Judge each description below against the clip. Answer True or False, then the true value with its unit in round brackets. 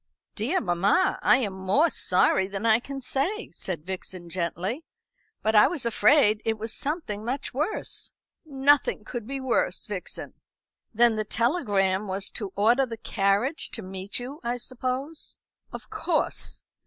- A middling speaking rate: True (150 wpm)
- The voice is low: False (230 Hz)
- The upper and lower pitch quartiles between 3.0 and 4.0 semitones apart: False (5.4 semitones)